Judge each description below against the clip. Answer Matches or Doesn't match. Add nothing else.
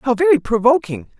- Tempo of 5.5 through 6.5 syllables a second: Matches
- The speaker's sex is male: Doesn't match